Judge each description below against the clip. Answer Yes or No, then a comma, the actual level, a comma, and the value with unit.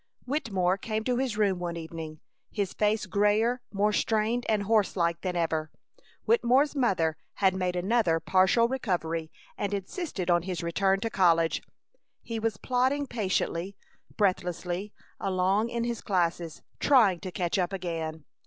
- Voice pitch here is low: No, high, 195 Hz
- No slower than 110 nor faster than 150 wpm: Yes, average, 145 wpm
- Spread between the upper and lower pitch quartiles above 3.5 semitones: Yes, average, 4.5 semitones